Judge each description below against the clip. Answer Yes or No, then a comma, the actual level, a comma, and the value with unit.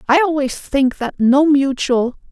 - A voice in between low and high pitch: No, very high, 275 Hz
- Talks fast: No, average, 155 wpm